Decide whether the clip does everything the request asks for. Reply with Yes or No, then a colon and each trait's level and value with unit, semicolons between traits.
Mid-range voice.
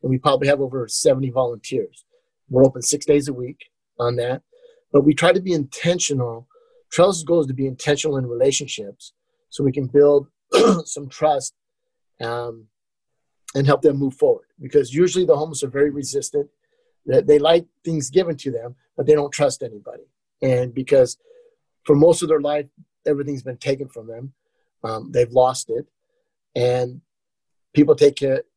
Yes: medium, 145 Hz